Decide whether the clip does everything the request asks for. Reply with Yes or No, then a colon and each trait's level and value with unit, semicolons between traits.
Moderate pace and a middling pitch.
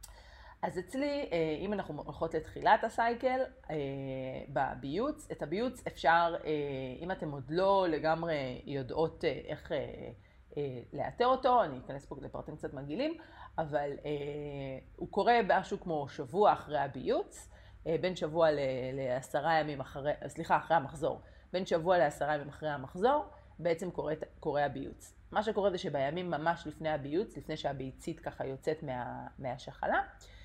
Yes: average, 130 wpm; medium, 155 Hz